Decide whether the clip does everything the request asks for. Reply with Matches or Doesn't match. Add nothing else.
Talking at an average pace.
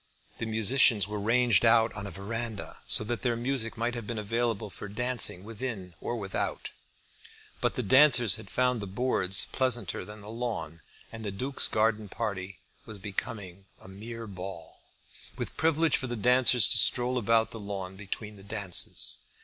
Matches